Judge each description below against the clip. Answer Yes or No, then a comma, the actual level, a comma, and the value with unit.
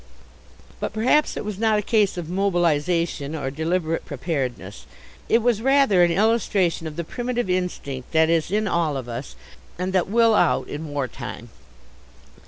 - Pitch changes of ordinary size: No, wide, 5.8 semitones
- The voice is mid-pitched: Yes, medium, 175 Hz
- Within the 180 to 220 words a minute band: No, average, 165 wpm